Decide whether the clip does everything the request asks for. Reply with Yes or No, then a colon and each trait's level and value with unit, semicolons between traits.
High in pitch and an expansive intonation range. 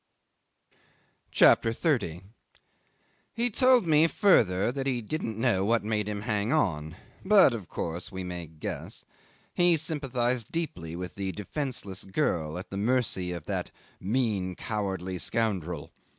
No: low, 105 Hz; wide, 6.5 semitones